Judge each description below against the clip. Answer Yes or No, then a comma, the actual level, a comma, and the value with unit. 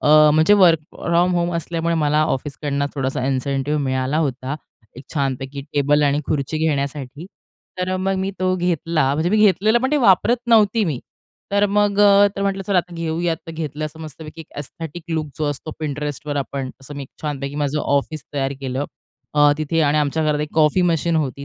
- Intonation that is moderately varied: Yes, average, 3.6 semitones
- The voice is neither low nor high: Yes, medium, 155 Hz